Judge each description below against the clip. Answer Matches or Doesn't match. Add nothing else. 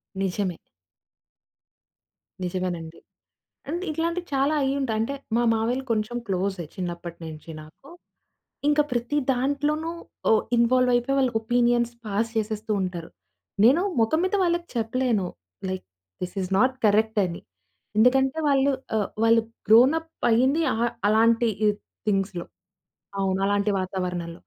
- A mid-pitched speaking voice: Doesn't match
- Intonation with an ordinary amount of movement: Doesn't match